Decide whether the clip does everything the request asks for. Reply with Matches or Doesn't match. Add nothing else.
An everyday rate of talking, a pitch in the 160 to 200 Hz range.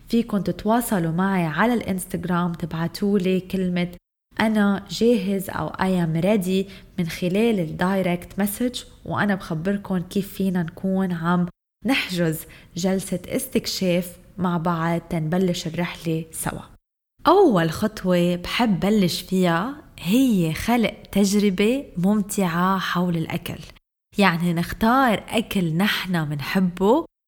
Matches